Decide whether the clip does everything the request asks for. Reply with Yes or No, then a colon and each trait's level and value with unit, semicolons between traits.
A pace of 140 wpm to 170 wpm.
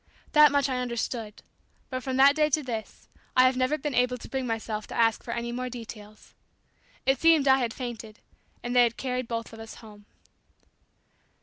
No: average, 185 wpm